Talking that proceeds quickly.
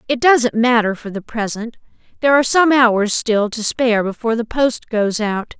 No: average, 195 wpm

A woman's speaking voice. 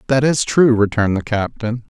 No: male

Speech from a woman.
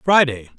No: male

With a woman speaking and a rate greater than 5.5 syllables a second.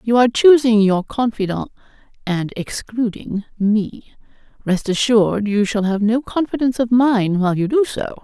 No: female; 4.9 syllables/s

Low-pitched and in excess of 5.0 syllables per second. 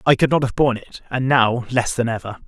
Yes: low, 120 Hz; 5.9 syllables/s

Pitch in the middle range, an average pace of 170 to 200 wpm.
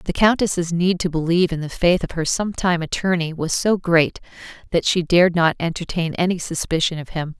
Yes: medium, 170 Hz; average, 195 wpm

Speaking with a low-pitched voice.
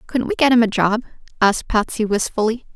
No: high, 220 Hz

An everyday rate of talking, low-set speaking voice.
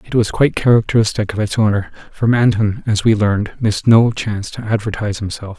Yes: average, 195 wpm; low, 110 Hz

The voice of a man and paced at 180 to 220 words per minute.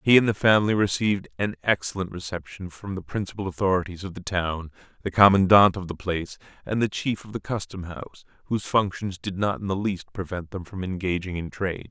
Yes: male; average, 200 wpm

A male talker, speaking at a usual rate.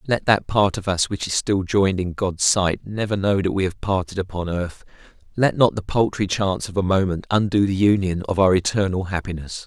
No: male; fast, 215 wpm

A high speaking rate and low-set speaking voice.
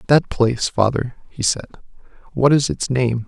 No: average, 165 wpm; low, 125 Hz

